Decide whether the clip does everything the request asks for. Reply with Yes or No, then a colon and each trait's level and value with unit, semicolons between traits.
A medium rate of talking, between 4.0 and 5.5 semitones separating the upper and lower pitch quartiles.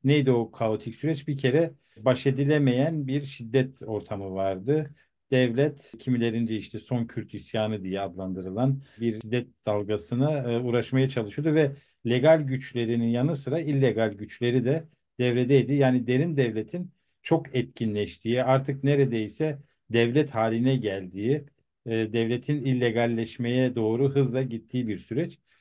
No: average, 120 wpm; average, 3.6 semitones